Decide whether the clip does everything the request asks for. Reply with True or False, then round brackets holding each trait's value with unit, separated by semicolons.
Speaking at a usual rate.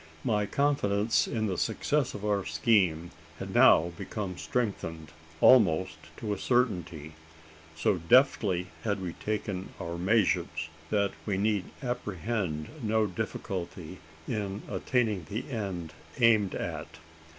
False (125 wpm)